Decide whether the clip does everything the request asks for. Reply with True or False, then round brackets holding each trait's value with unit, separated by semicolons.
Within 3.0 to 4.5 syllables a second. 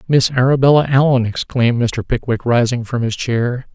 False (5.1 syllables/s)